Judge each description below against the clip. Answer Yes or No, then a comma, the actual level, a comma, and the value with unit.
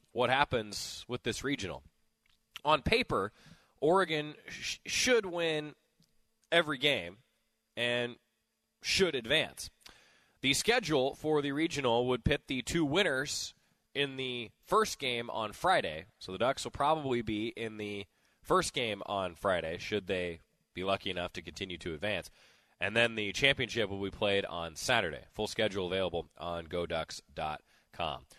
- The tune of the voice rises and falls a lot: Yes, wide, 6.7 semitones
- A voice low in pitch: Yes, low, 115 Hz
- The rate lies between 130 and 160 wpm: Yes, average, 140 wpm